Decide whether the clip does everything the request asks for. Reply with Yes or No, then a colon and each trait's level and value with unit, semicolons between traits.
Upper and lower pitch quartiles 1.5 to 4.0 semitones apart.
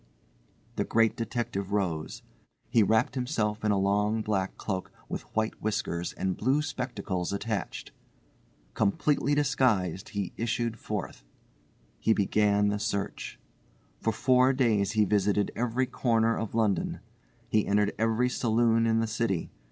Yes: narrow, 2.6 semitones